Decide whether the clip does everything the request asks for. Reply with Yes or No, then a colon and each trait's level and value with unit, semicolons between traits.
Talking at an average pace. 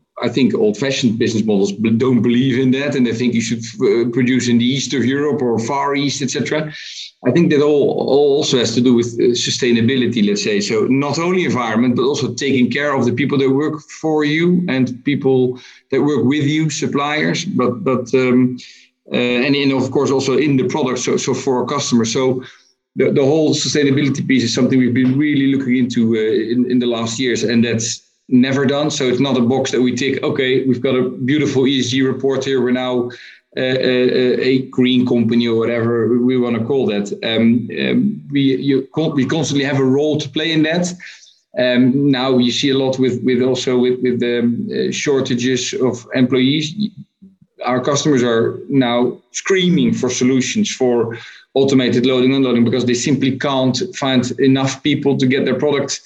Yes: average, 195 wpm